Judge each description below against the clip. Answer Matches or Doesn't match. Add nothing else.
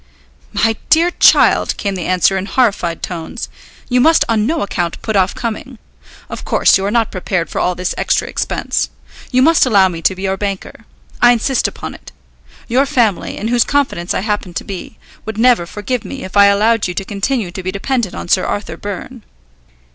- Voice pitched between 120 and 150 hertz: Doesn't match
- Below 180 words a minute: Doesn't match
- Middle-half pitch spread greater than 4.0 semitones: Matches